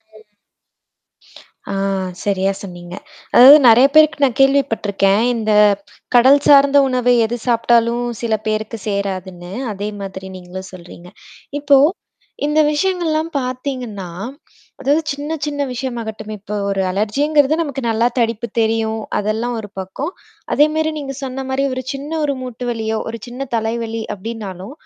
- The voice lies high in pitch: Yes, high, 235 Hz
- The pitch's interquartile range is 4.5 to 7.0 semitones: Yes, average, 4.9 semitones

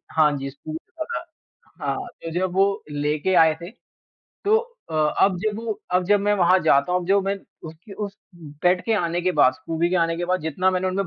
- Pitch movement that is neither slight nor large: Yes, average, 3.4 semitones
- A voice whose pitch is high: No, medium, 180 Hz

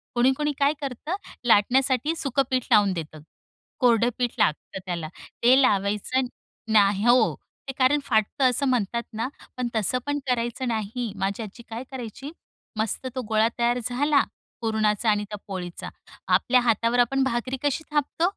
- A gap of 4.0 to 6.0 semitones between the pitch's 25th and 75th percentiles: No, average, 3.5 semitones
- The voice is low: No, high, 240 Hz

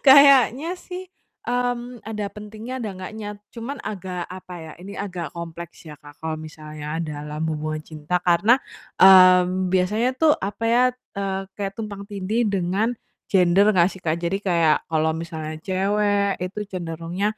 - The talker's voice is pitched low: No, medium, 185 Hz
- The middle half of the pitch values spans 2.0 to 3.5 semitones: No, average, 4.0 semitones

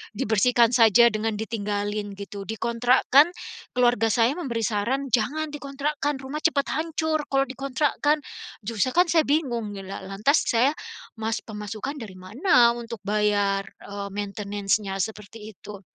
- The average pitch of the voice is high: Yes, high, 230 Hz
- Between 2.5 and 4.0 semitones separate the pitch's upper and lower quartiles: No, average, 5.0 semitones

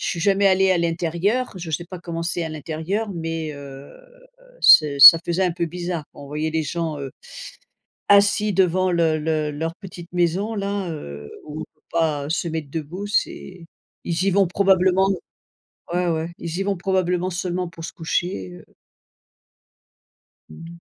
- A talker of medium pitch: Yes, medium, 170 Hz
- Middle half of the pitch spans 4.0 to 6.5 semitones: No, average, 2.8 semitones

